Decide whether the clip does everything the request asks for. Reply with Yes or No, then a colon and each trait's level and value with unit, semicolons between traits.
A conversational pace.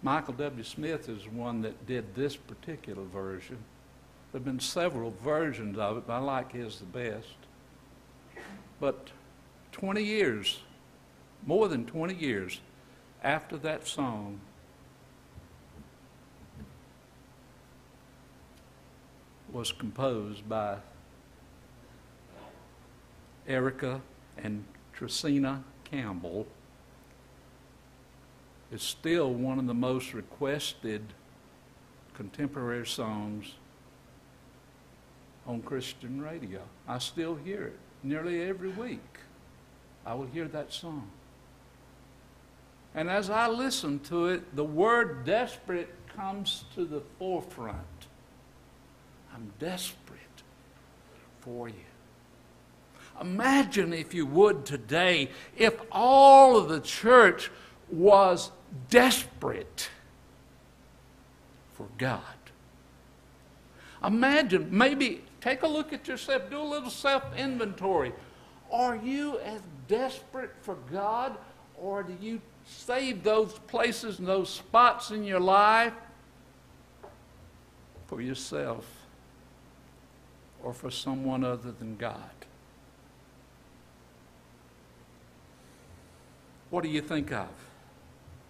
No: slow, 95 wpm